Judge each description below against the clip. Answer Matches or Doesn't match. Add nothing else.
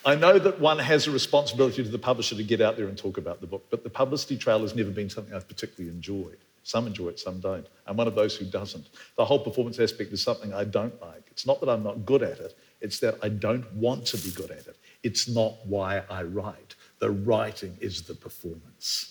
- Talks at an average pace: Doesn't match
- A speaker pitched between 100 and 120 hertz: Matches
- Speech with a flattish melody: Doesn't match